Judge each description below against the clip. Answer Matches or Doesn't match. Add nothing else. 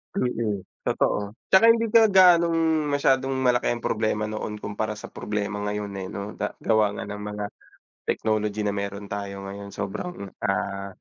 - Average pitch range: Matches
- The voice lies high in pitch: Doesn't match